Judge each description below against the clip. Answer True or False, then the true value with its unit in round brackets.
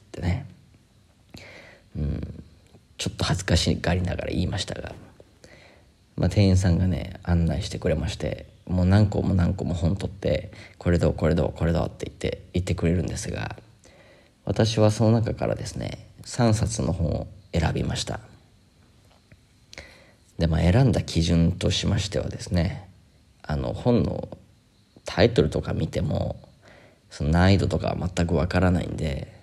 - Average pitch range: True (3.8 semitones)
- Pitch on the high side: False (90 Hz)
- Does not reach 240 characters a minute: False (280 characters per minute)